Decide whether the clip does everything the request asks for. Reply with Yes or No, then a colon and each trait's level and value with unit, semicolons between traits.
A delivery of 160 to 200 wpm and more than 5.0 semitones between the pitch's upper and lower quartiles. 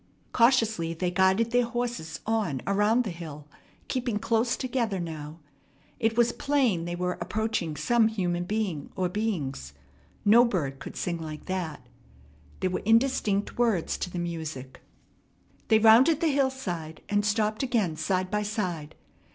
No: average, 145 wpm; wide, 5.4 semitones